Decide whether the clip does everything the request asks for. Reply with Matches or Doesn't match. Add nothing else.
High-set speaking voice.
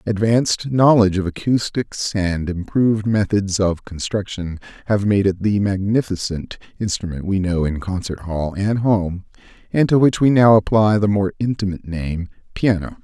Doesn't match